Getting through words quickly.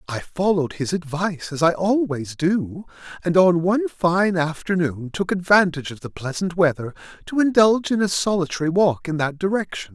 No: average, 170 wpm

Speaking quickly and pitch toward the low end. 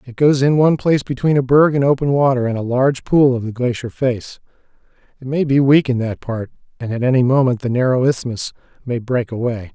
Yes: fast, 215 wpm; low, 130 Hz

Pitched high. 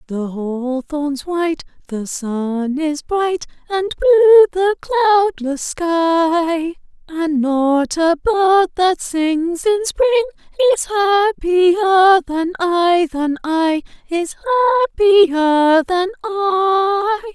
Yes: very high, 340 Hz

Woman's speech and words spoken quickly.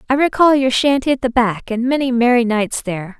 Yes: female; fast, 225 wpm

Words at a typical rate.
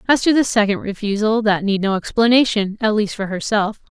Yes: average, 195 wpm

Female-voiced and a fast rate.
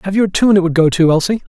No: male; fast, 350 wpm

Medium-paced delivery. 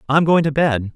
No: fast, 255 wpm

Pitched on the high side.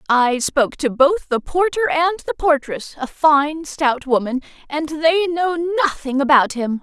Yes: very high, 300 Hz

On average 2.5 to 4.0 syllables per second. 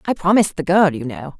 No: 6.5 syllables/s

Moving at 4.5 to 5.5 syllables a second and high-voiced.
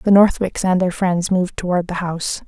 No: 5.4 syllables/s; medium, 180 Hz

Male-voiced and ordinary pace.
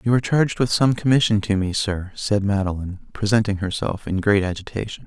Yes: male; average, 190 wpm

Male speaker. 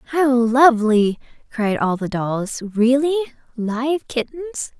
No: female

